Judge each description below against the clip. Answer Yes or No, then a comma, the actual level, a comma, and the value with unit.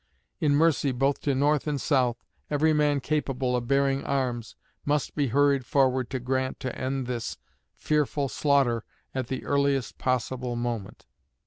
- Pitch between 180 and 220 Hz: No, low, 135 Hz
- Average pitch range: No, narrow, 2.2 semitones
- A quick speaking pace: No, average, 150 wpm